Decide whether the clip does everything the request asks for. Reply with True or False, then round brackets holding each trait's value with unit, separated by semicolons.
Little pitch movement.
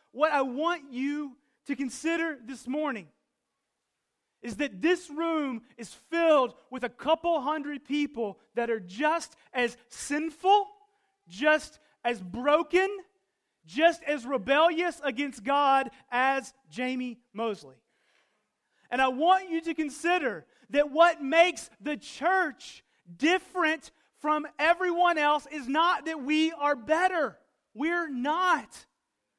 False (4.2 semitones)